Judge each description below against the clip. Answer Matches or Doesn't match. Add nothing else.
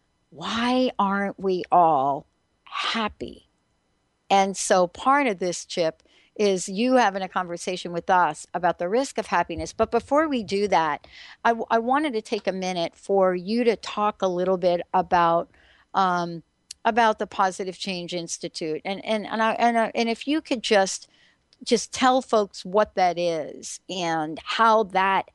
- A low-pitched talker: Doesn't match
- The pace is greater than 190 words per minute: Doesn't match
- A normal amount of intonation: Matches